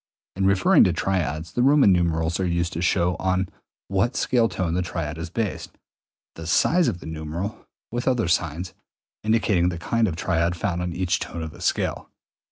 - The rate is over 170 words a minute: Yes, average, 185 wpm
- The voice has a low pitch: Yes, very low, 90 Hz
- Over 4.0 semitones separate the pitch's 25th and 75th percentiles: No, average, 2.8 semitones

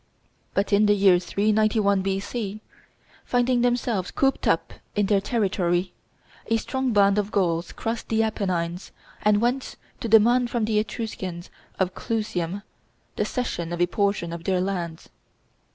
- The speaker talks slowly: No, average, 145 wpm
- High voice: Yes, high, 205 Hz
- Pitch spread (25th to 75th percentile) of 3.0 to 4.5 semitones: Yes, average, 3.5 semitones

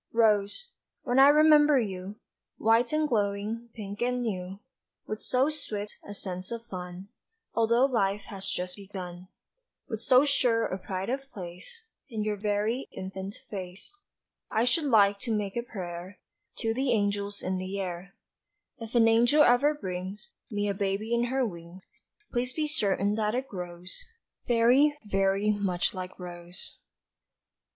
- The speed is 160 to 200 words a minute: No, average, 150 wpm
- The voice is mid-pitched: No, high, 210 Hz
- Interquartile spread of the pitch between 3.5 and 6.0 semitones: Yes, average, 4.0 semitones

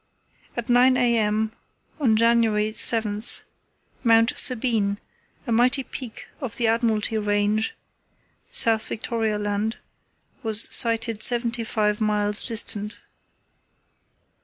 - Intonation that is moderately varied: No, narrow, 1.9 semitones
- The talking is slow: Yes, slow, 100 wpm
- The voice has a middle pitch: No, high, 225 Hz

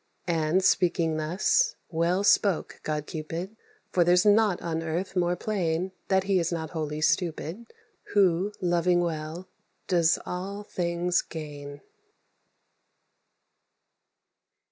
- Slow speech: Yes, slow, 110 wpm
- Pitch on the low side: No, medium, 175 Hz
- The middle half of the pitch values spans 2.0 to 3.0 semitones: Yes, average, 2.7 semitones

